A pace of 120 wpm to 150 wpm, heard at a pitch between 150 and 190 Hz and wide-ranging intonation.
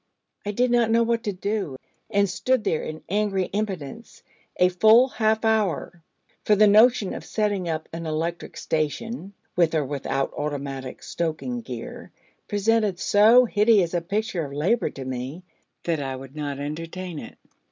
No: average, 160 wpm; medium, 185 Hz; wide, 5.8 semitones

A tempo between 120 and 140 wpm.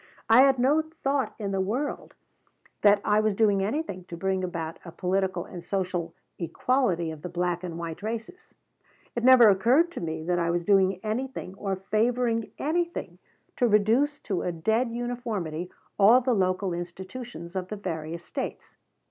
No: average, 165 wpm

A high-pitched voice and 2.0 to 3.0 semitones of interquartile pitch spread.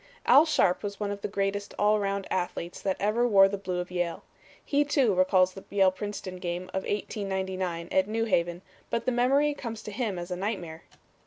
Yes: high, 195 Hz; average, 2.7 semitones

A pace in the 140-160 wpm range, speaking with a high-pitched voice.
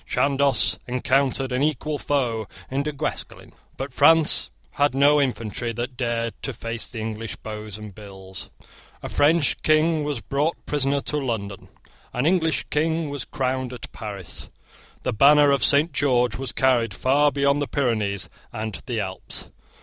No: average, 155 wpm; low, 130 Hz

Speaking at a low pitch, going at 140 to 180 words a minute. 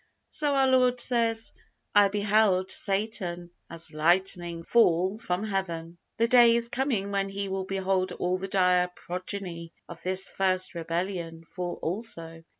No: high, 190 Hz; average, 145 wpm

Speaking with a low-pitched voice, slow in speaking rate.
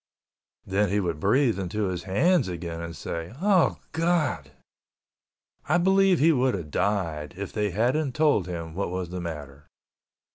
No: low, 100 Hz; average, 150 wpm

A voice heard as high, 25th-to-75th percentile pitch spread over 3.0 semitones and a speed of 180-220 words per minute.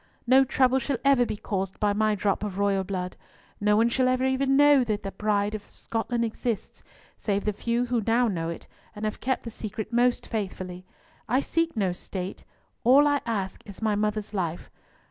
Yes: high, 215 Hz; average, 3.7 semitones; average, 190 wpm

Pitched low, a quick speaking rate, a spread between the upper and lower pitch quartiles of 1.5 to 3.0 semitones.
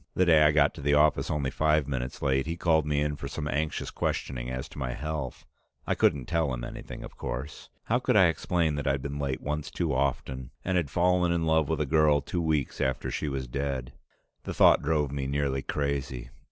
Yes: very low, 70 Hz; fast, 220 wpm; narrow, 2.6 semitones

